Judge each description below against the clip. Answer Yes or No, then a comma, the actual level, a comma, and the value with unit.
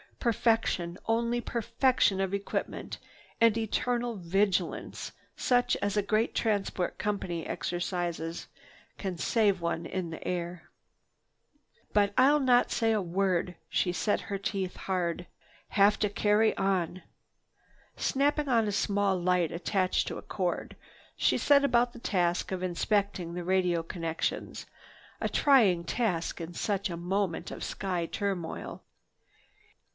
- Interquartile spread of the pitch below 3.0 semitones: No, average, 4.1 semitones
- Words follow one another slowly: Yes, slow, 130 wpm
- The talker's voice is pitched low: No, high, 195 Hz